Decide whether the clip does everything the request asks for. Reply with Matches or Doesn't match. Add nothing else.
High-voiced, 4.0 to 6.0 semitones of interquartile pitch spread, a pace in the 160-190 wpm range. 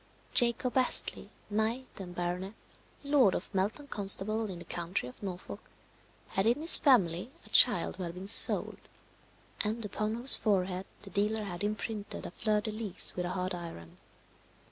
Doesn't match